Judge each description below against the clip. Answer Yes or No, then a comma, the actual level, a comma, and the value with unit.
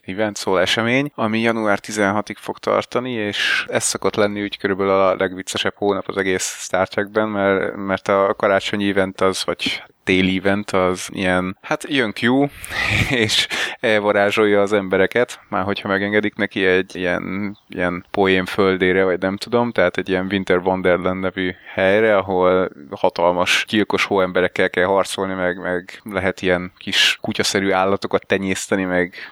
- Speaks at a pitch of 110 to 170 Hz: No, very low, 95 Hz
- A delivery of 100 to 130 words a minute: No, average, 145 wpm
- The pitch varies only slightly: Yes, narrow, 1.8 semitones